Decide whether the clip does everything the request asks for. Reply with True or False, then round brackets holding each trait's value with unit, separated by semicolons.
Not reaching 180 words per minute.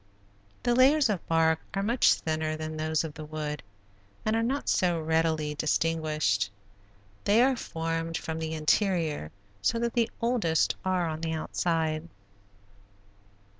True (140 wpm)